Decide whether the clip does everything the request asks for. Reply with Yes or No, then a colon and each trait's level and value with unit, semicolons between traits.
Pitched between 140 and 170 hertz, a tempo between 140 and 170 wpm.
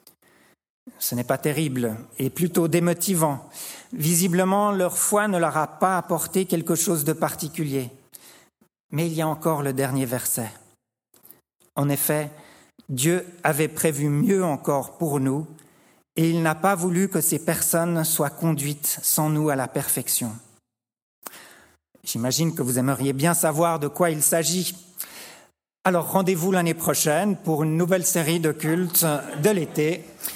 Yes: medium, 160 Hz; slow, 145 wpm